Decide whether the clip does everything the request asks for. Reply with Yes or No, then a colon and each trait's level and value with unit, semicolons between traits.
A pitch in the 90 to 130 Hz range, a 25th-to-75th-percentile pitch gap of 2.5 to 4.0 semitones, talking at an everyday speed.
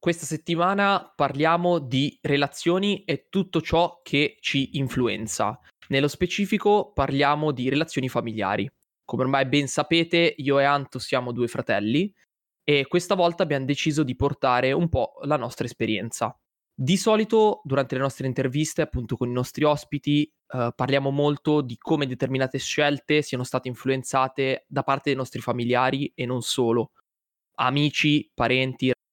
No: medium, 140 Hz; average, 3.4 semitones; average, 145 wpm